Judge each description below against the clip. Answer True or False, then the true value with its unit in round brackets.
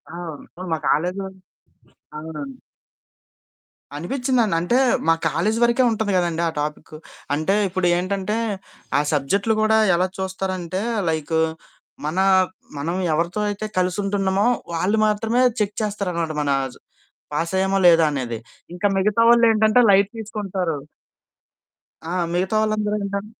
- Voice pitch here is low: False (190 Hz)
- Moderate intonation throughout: True (4.1 semitones)